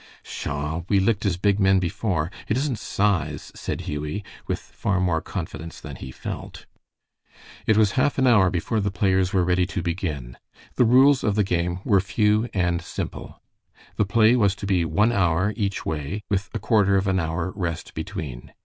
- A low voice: Yes, very low, 95 Hz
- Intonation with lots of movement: No, average, 3.5 semitones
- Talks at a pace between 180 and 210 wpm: Yes, average, 185 wpm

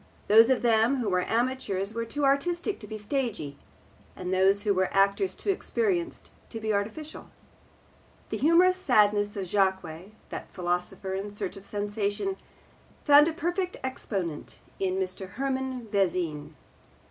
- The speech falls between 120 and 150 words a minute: Yes, average, 145 wpm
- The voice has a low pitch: No, high, 210 Hz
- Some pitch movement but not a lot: No, wide, 6.2 semitones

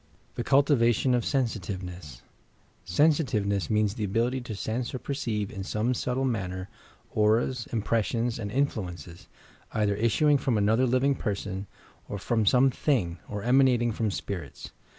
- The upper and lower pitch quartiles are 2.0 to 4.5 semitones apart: Yes, average, 4.0 semitones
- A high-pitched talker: No, low, 115 Hz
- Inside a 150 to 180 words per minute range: No, average, 140 wpm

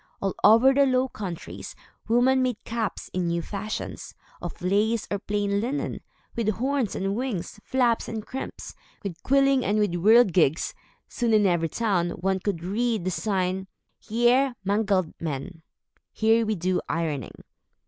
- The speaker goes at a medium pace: Yes, average, 150 wpm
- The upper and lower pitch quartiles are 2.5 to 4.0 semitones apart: No, average, 4.5 semitones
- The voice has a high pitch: Yes, high, 210 Hz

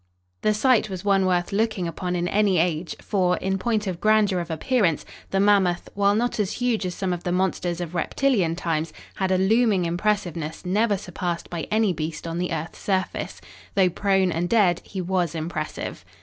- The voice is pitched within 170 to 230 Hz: Yes, medium, 185 Hz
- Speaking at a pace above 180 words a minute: Yes, average, 190 wpm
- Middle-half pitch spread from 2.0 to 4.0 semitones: Yes, average, 3.0 semitones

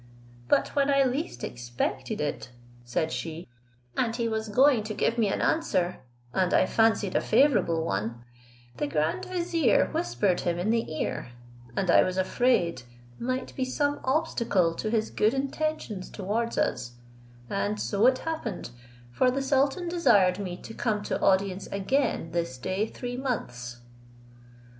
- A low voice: No, high, 210 Hz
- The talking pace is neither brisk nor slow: Yes, average, 150 wpm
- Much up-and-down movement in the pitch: Yes, wide, 7.4 semitones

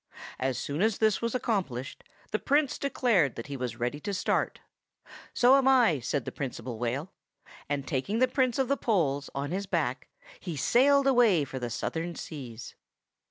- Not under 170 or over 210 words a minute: Yes, average, 175 wpm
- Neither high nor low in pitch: Yes, medium, 170 Hz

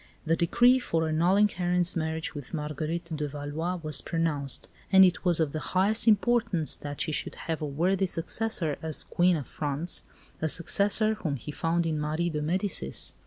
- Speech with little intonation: No, average, 3.2 semitones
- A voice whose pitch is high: No, medium, 165 Hz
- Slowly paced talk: No, average, 175 wpm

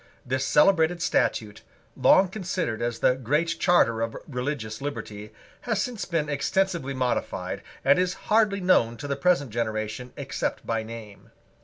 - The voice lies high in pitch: No, medium, 140 Hz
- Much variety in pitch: Yes, wide, 7.5 semitones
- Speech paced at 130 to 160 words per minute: Yes, average, 145 wpm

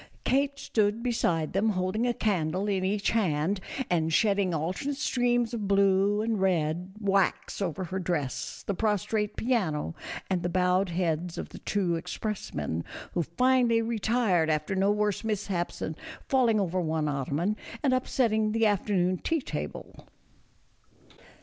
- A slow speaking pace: No, average, 145 wpm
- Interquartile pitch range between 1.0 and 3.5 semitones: No, average, 4.2 semitones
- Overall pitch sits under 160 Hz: No, high, 195 Hz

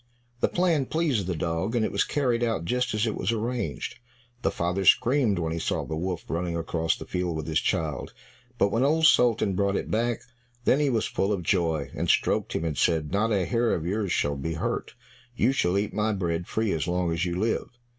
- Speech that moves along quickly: Yes, fast, 225 wpm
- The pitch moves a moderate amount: No, wide, 5.7 semitones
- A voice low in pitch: Yes, very low, 95 Hz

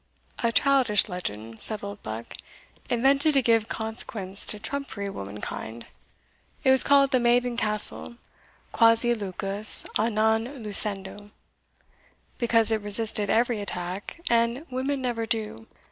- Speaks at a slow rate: Yes, slow, 120 wpm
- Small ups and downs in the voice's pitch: No, average, 3.1 semitones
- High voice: Yes, high, 220 Hz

